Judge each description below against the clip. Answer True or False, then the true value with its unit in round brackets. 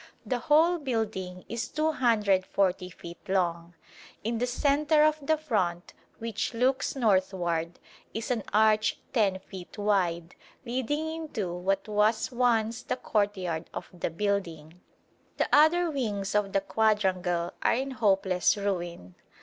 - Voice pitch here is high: True (210 Hz)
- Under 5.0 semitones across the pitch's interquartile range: False (5.3 semitones)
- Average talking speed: False (130 wpm)